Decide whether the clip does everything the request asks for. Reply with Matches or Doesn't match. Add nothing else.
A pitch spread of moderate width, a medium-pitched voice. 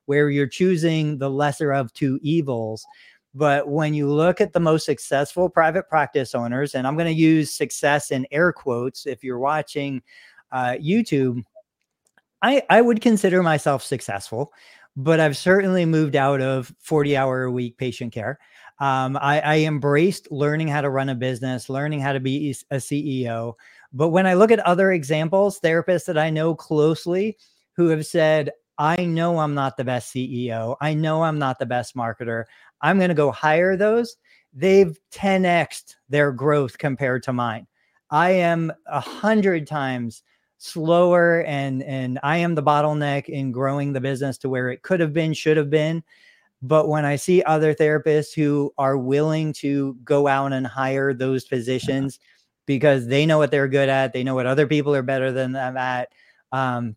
Matches